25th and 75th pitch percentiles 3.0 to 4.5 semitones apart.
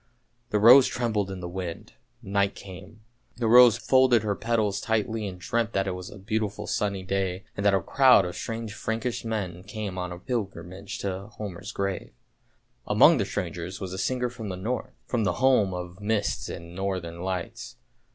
Yes: average, 3.3 semitones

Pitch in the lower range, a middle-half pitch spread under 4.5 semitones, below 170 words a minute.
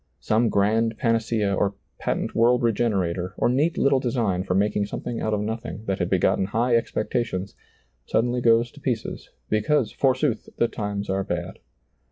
Yes: low, 110 Hz; average, 3.0 semitones; average, 160 wpm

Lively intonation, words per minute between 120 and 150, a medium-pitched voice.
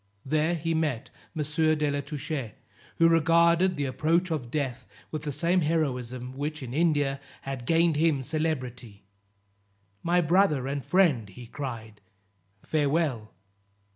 No: average, 4.3 semitones; slow, 135 wpm; medium, 150 Hz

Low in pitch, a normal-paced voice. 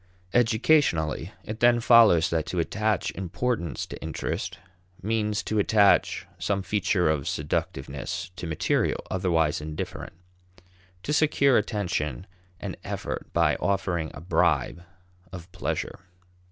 No: very low, 95 Hz; slow, 115 wpm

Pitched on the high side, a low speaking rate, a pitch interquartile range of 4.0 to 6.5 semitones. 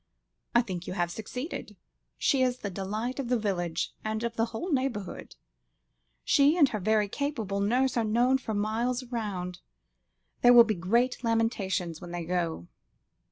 No: high, 220 Hz; average, 160 wpm; average, 4.5 semitones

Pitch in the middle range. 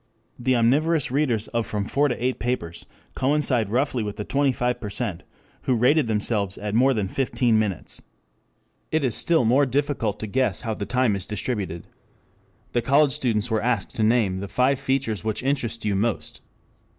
No: low, 120 Hz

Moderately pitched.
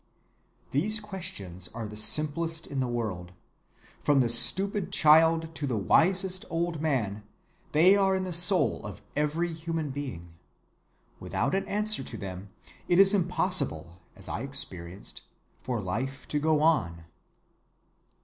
Yes: medium, 150 Hz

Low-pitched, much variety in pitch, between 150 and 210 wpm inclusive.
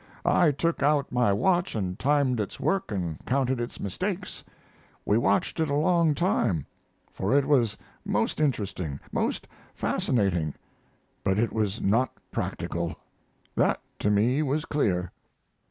No: low, 125 Hz; wide, 6.9 semitones; average, 140 wpm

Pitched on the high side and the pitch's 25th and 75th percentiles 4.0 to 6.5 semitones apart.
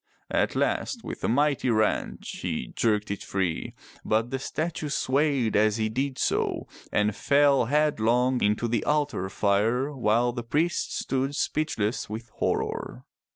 No: low, 120 Hz; average, 4.6 semitones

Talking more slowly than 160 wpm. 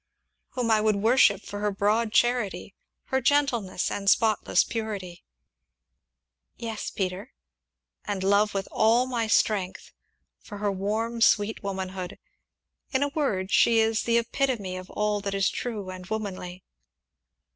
Yes: slow, 135 wpm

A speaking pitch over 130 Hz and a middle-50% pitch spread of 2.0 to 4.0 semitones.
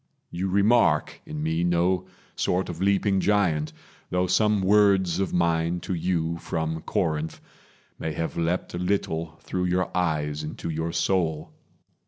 No: very low, 85 Hz; narrow, 2.6 semitones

